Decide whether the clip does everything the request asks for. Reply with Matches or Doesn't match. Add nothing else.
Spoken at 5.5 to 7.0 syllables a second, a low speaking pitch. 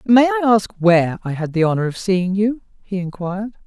Doesn't match